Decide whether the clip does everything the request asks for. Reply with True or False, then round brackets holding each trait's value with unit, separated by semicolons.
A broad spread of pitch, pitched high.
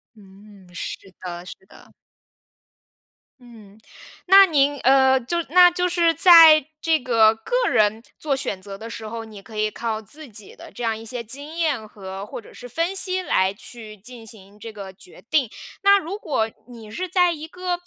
True (7.2 semitones; 235 Hz)